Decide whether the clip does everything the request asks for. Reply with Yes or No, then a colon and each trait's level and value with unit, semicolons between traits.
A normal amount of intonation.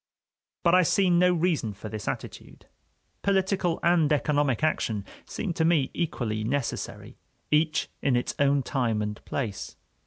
No: wide, 6.6 semitones